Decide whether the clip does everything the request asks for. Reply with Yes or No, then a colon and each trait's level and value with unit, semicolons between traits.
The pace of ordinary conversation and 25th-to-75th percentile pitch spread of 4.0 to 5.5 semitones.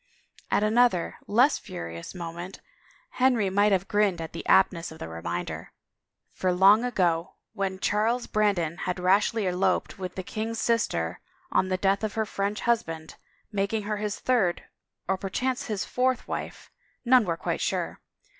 No: average, 160 wpm; average, 3.5 semitones